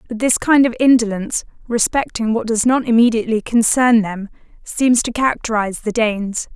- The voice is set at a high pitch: Yes, high, 230 Hz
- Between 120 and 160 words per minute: Yes, average, 155 wpm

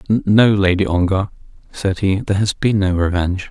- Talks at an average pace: Yes, average, 170 wpm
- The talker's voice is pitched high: No, very low, 95 Hz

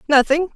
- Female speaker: Yes, female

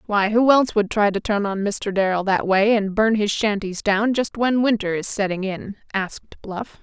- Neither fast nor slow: No, fast, 220 wpm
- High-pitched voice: Yes, high, 205 Hz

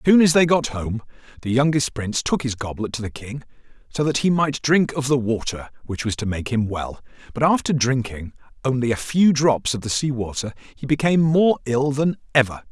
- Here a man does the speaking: Yes, male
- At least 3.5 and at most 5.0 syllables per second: No, 5.4 syllables/s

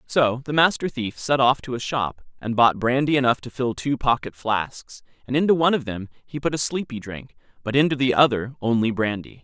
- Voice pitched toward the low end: Yes, low, 125 Hz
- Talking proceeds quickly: Yes, fast, 215 wpm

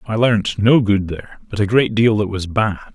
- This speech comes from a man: Yes, male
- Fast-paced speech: Yes, fast, 245 wpm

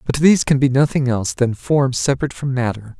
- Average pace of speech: No, fast, 220 wpm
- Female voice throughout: No, male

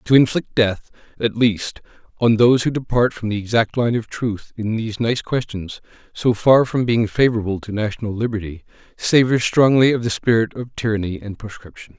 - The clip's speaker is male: Yes, male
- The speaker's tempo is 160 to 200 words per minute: Yes, average, 180 wpm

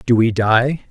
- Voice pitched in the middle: No, low, 120 Hz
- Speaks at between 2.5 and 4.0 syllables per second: Yes, 3.7 syllables/s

